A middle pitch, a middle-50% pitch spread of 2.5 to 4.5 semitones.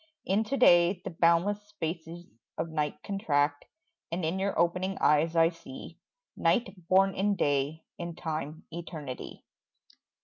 Yes: medium, 170 Hz; average, 3.3 semitones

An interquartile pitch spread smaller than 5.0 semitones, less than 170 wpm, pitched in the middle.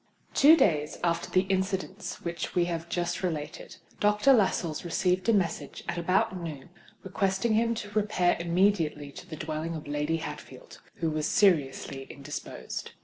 Yes: average, 3.6 semitones; average, 150 wpm; medium, 175 Hz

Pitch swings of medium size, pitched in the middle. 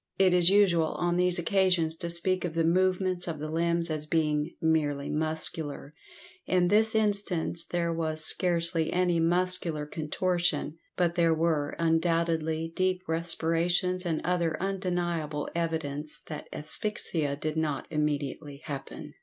No: narrow, 2.3 semitones; medium, 165 Hz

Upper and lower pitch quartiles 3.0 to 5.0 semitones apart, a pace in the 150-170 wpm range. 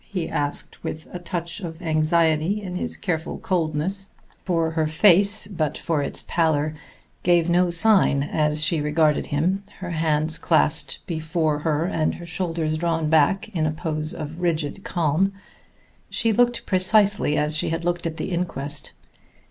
No: narrow, 2.6 semitones; average, 155 wpm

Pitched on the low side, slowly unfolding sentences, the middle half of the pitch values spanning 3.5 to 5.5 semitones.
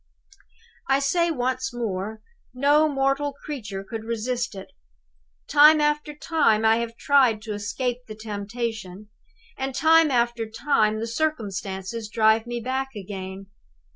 No: high, 235 Hz; slow, 130 wpm; average, 4.3 semitones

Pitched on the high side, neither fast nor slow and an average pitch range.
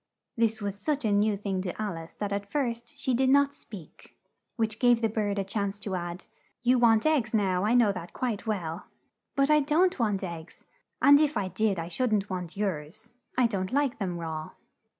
No: high, 210 Hz; fast, 210 wpm; average, 4.4 semitones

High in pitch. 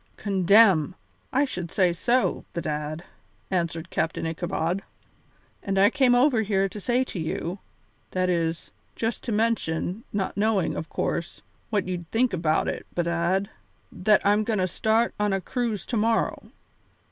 Yes: high, 195 Hz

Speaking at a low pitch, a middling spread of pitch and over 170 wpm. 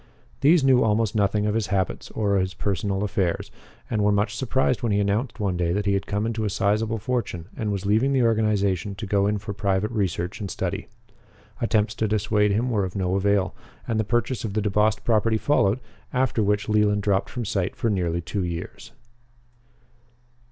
No: low, 105 Hz; narrow, 2.1 semitones; average, 200 wpm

